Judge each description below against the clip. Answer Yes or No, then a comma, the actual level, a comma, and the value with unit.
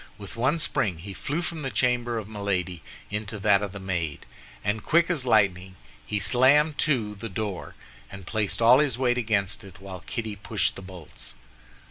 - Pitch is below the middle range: Yes, low, 105 Hz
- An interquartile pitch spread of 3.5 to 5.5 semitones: Yes, average, 4.2 semitones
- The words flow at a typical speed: Yes, average, 180 wpm